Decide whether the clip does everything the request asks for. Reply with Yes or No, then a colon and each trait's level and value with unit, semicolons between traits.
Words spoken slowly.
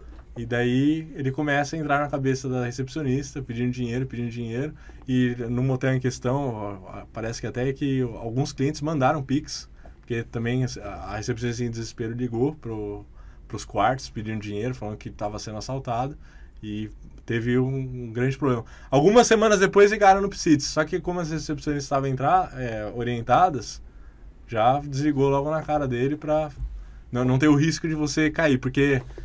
No: average, 165 wpm